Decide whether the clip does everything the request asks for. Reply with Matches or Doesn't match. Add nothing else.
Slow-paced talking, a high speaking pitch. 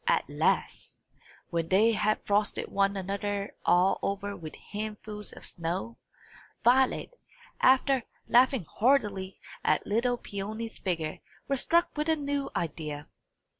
Matches